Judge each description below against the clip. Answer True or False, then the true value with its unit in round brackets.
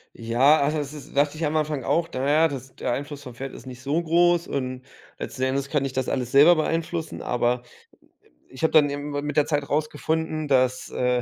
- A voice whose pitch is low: False (145 Hz)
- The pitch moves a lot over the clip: False (3.1 semitones)